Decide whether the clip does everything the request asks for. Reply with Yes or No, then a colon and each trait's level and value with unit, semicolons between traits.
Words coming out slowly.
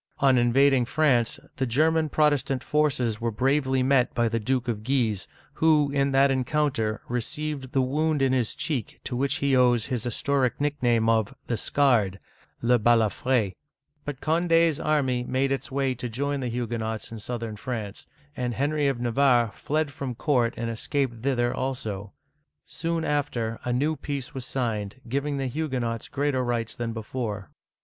No: average, 170 wpm